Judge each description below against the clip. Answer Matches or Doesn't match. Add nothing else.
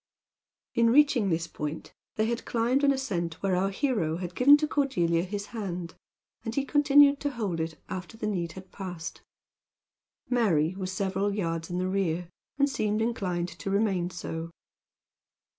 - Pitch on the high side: Matches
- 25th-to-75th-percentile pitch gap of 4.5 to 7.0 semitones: Matches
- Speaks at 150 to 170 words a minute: Matches